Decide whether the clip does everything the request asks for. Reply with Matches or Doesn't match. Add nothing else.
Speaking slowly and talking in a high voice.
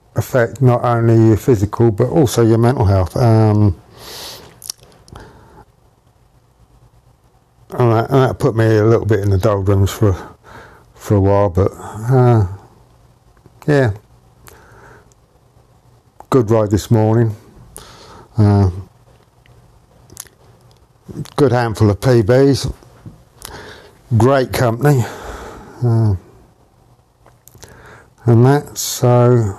Doesn't match